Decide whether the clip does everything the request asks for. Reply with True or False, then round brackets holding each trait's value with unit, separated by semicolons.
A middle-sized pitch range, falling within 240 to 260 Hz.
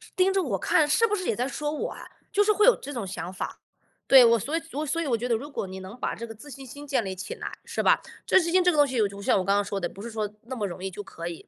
False (7.1 semitones; 245 Hz)